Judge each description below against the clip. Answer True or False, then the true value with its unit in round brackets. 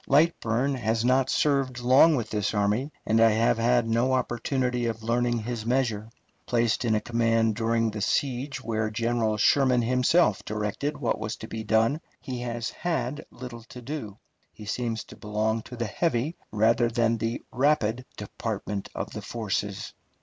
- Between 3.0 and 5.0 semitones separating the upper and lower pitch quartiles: False (2.4 semitones)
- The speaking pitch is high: False (115 Hz)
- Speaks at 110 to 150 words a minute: False (165 wpm)